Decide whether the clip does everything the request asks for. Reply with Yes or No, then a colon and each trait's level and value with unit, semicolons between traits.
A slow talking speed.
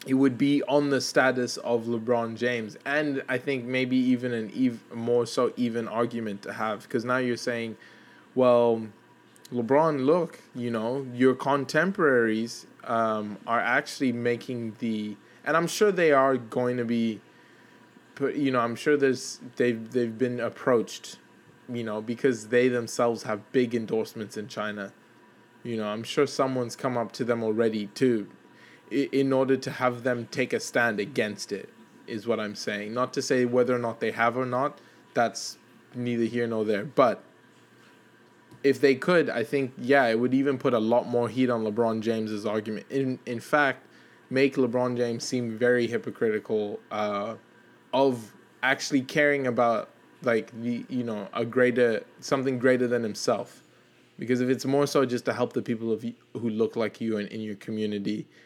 No: average, 170 wpm